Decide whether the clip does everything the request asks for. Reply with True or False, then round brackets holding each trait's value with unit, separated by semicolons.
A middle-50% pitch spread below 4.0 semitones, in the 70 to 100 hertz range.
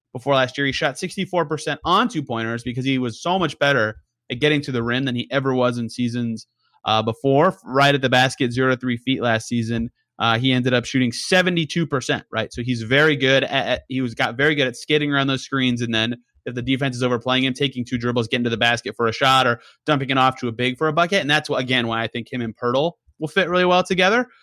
False (3.1 semitones; 130 Hz)